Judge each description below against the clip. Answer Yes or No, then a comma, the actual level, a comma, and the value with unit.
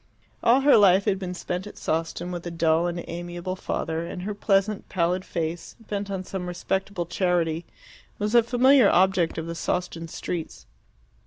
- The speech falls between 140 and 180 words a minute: Yes, average, 170 wpm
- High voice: No, medium, 180 Hz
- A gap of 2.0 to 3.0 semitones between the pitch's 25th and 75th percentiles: Yes, average, 2.7 semitones